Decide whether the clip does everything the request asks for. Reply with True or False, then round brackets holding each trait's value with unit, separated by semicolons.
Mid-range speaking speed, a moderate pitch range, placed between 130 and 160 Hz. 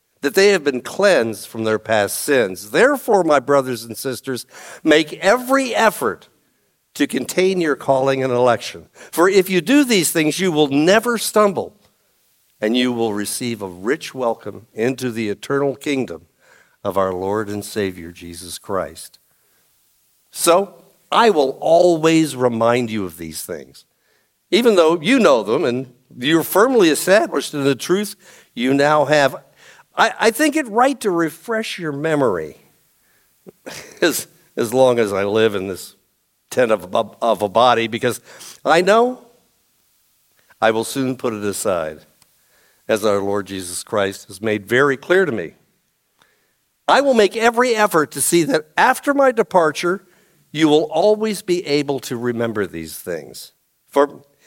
False (150 wpm; 8.1 semitones; 140 Hz)